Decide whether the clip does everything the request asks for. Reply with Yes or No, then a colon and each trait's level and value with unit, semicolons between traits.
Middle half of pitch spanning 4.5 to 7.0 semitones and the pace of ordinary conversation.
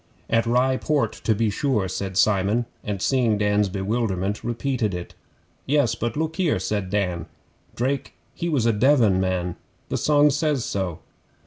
Yes: average, 5.1 semitones; average, 155 wpm